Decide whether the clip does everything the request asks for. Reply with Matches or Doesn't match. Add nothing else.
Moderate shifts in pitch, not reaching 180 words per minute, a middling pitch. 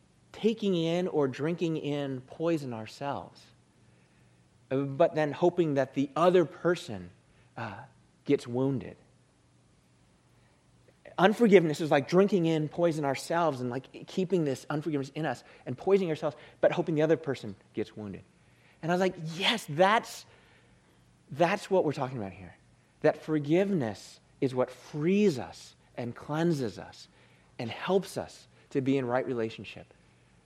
Doesn't match